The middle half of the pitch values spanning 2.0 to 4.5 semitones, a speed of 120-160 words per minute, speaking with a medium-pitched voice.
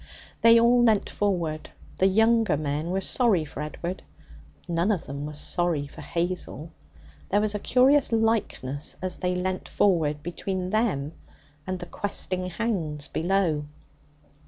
No: average, 5.2 semitones; average, 140 wpm; medium, 180 Hz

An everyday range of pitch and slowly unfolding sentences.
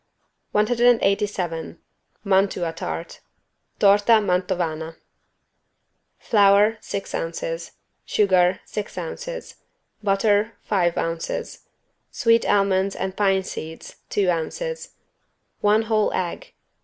Yes: average, 3.1 semitones; slow, 85 wpm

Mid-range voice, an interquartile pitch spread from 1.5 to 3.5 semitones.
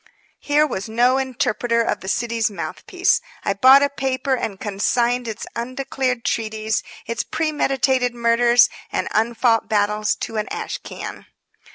No: high, 235 Hz; average, 3.0 semitones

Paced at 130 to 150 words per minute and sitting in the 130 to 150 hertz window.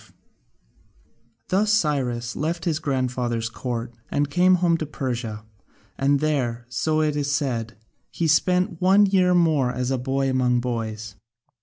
Yes: average, 145 wpm; low, 135 Hz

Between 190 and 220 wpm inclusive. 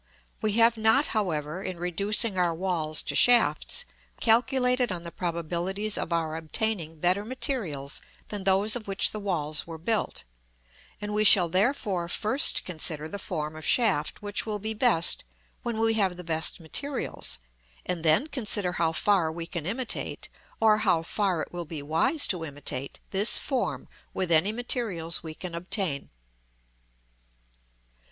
No: average, 155 wpm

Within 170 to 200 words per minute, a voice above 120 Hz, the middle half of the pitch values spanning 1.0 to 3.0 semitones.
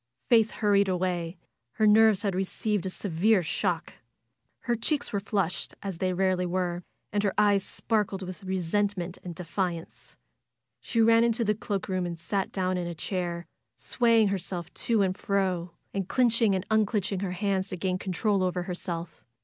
Yes: average, 180 wpm; high, 190 Hz; narrow, 2.6 semitones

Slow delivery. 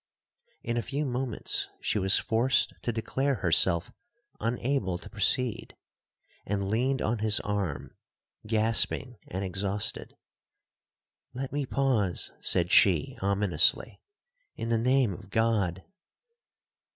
Yes: slow, 115 wpm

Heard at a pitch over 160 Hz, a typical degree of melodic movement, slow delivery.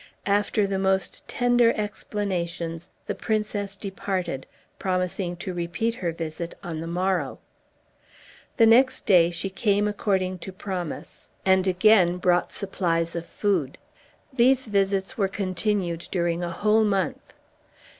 Yes: high, 190 Hz; average, 3.0 semitones; slow, 125 wpm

